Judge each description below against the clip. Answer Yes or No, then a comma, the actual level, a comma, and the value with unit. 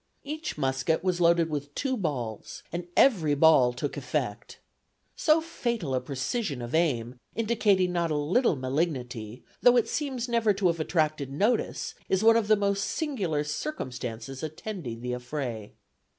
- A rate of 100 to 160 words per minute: Yes, average, 150 wpm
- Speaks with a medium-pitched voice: Yes, medium, 160 Hz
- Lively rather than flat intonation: Yes, wide, 8.4 semitones